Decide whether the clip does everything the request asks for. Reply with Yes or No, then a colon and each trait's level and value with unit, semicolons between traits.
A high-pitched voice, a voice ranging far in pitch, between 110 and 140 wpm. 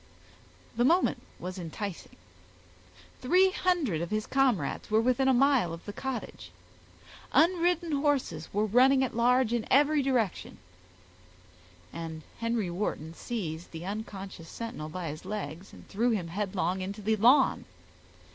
Yes: high, 215 Hz; wide, 6.4 semitones; slow, 135 wpm